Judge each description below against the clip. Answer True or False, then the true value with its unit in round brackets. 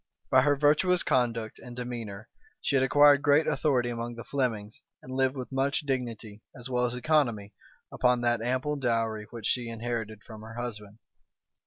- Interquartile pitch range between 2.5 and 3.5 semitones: True (2.8 semitones)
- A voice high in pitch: False (120 Hz)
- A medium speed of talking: True (170 wpm)